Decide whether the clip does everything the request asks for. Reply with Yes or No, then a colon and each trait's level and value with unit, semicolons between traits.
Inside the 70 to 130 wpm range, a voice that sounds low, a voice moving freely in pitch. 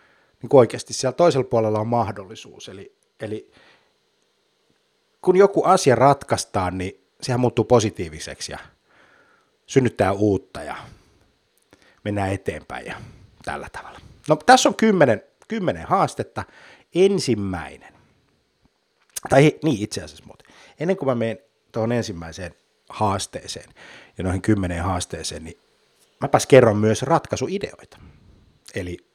Yes: average, 110 wpm; low, 115 Hz; wide, 7.2 semitones